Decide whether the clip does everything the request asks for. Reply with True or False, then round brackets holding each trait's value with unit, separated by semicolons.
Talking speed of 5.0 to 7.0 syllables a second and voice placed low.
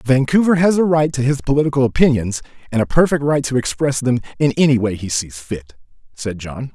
True (5.7 syllables/s; 130 Hz)